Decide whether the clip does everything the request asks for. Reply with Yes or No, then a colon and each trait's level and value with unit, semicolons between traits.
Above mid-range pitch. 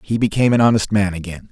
No: low, 105 Hz